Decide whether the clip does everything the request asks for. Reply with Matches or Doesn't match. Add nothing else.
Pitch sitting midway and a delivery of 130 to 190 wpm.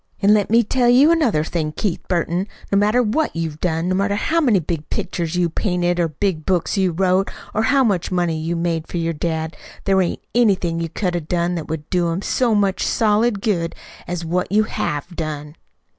Doesn't match